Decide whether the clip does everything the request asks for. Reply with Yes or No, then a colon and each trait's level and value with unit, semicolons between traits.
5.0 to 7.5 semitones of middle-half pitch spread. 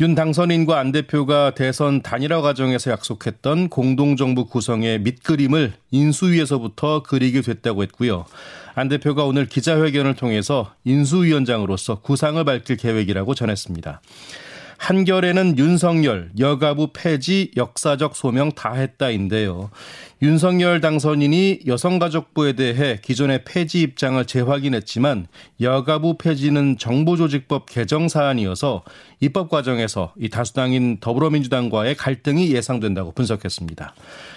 No: average, 4.2 semitones